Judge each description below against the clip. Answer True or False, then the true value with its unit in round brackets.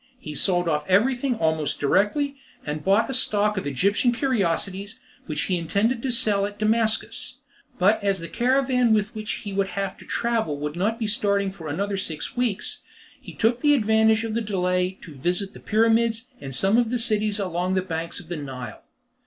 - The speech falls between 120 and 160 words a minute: False (185 wpm)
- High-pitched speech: True (205 Hz)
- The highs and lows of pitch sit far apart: False (4.1 semitones)